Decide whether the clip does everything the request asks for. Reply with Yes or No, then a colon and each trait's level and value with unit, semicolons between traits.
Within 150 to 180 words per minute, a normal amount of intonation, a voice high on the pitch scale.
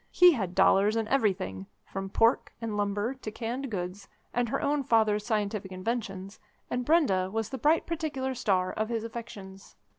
Yes: average, 170 wpm; average, 4.1 semitones; high, 220 Hz